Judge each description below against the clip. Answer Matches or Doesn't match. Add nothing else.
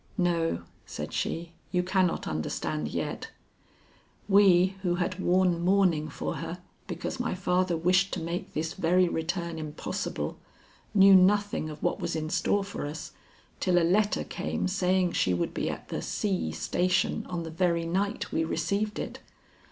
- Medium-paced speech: Matches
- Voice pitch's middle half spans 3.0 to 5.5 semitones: Doesn't match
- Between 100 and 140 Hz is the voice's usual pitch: Doesn't match